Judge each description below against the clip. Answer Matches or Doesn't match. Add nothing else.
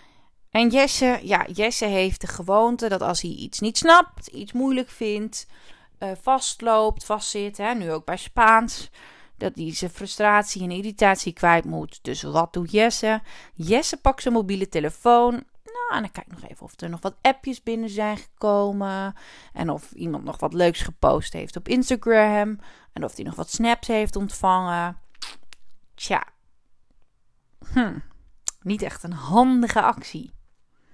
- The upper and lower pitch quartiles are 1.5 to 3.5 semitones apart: Doesn't match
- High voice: Matches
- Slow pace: Doesn't match